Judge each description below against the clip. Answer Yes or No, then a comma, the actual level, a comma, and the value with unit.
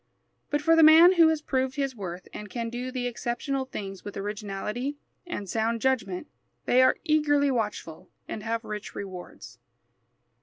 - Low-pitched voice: No, high, 245 Hz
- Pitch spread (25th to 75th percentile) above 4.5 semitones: Yes, average, 5.3 semitones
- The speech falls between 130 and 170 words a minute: Yes, average, 160 wpm